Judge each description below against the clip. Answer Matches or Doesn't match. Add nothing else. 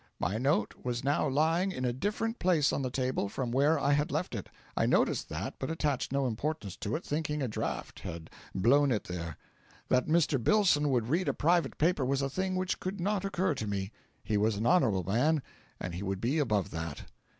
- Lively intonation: Matches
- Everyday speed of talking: Doesn't match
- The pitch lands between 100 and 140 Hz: Matches